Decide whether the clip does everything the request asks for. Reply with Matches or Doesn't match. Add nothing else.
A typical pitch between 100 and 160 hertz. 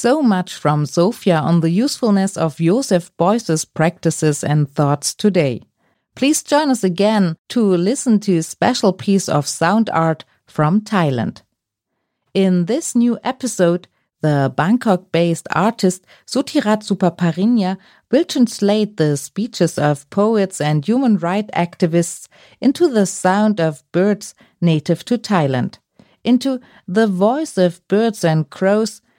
Doesn't match